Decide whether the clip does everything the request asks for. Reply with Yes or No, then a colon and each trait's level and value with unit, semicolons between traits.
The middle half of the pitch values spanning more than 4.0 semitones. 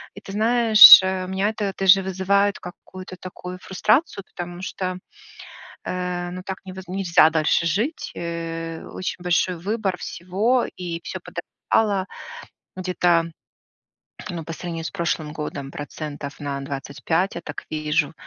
No: average, 2.7 semitones